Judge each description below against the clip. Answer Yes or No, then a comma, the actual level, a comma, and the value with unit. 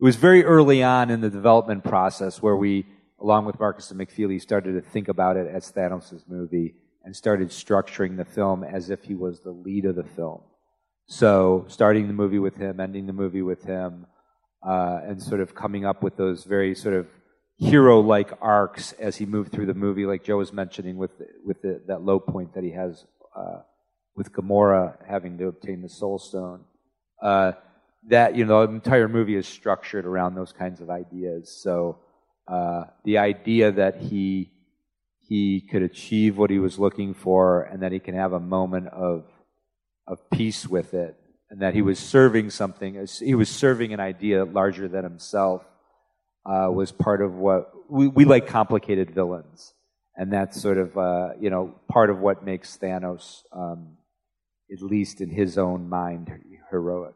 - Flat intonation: Yes, narrow, 1.9 semitones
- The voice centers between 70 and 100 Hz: Yes, very low, 95 Hz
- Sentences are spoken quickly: No, average, 185 wpm